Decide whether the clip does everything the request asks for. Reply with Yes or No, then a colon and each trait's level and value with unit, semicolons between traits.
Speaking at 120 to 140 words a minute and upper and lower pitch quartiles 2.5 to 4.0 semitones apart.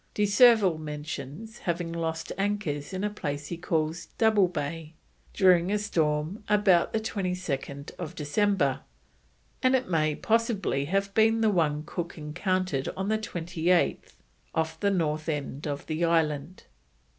No: slow, 135 wpm; average, 4.8 semitones